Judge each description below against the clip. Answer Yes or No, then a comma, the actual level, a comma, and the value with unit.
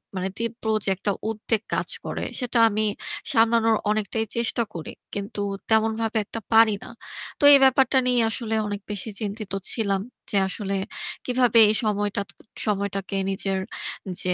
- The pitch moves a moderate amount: No, narrow, 2.3 semitones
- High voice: Yes, high, 215 Hz